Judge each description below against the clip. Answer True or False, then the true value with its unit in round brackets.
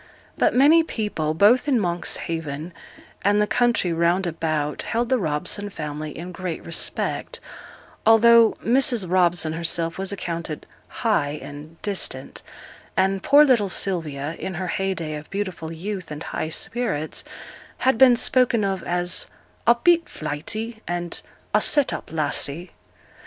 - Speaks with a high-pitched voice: False (180 Hz)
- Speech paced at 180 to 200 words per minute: False (135 wpm)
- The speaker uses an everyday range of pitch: False (5.7 semitones)